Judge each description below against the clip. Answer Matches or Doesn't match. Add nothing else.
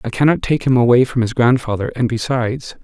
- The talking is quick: Matches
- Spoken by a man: Matches